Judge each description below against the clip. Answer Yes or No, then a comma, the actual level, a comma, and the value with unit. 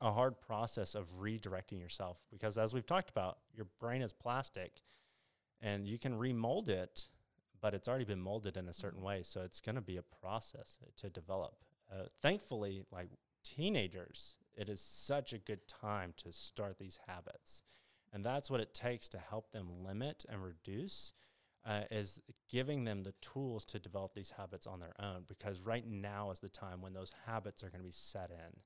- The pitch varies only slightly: No, average, 3.5 semitones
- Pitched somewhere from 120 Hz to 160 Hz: No, low, 105 Hz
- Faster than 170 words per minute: Yes, average, 195 wpm